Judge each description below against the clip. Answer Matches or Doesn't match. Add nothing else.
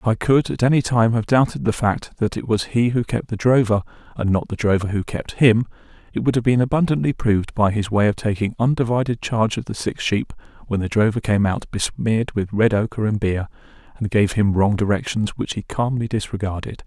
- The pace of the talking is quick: Matches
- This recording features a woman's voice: Doesn't match